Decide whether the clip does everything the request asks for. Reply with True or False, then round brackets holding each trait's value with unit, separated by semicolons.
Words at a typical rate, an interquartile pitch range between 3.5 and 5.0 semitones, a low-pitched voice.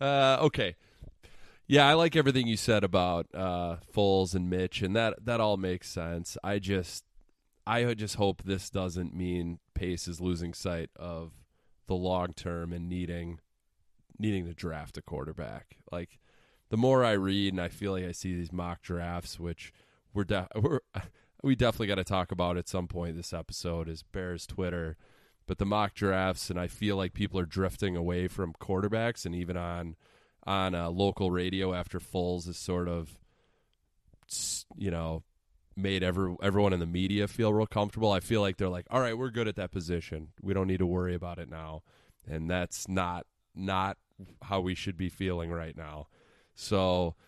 False (180 wpm; 2.5 semitones; 90 Hz)